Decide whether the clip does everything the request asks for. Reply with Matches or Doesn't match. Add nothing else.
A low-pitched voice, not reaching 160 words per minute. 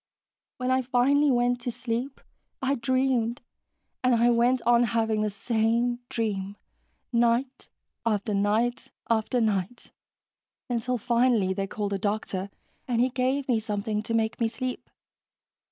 Doesn't match